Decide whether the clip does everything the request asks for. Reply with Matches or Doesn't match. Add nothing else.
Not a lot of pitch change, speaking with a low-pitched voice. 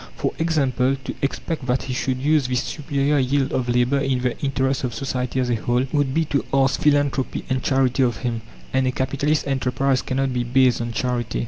Matches